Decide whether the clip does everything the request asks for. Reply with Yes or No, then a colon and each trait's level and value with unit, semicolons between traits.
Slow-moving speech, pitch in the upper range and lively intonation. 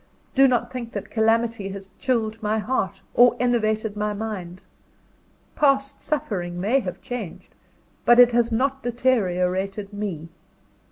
No: slow, 130 wpm; high, 220 Hz; average, 3.7 semitones